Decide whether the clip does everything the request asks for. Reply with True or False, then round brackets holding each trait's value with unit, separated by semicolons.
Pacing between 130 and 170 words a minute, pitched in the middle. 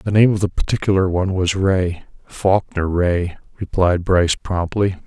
False (140 wpm; 90 Hz)